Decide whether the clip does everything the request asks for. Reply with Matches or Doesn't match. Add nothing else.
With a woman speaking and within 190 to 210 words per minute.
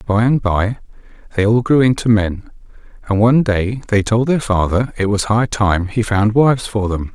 Doesn't match